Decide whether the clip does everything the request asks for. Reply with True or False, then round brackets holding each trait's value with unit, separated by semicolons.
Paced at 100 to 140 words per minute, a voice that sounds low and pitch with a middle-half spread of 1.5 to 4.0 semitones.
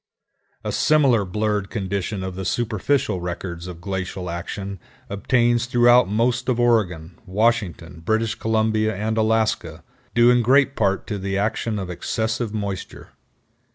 True (135 wpm; 110 Hz; 3.7 semitones)